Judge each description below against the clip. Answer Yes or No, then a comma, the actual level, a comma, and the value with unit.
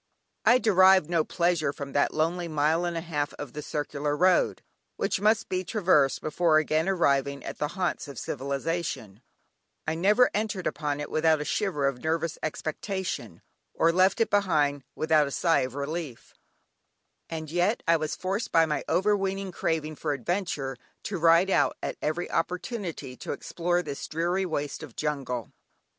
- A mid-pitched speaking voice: Yes, medium, 160 Hz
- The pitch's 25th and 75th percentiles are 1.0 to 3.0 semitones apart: No, average, 3.8 semitones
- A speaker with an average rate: Yes, average, 165 wpm